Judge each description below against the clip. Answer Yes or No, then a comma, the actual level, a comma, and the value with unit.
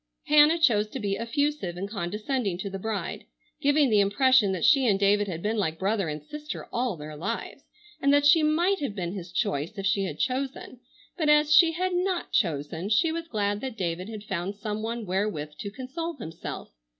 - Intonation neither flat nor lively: No, wide, 6.8 semitones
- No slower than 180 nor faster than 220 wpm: Yes, average, 200 wpm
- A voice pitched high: Yes, high, 215 Hz